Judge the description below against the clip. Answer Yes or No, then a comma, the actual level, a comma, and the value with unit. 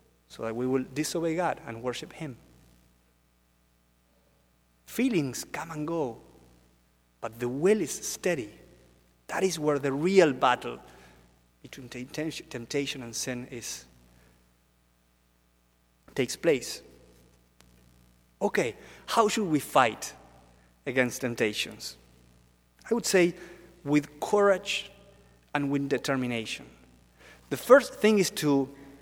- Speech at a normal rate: No, slow, 105 wpm